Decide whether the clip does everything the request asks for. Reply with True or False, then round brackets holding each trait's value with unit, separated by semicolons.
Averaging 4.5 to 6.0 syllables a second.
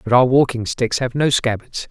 True (5.0 syllables/s)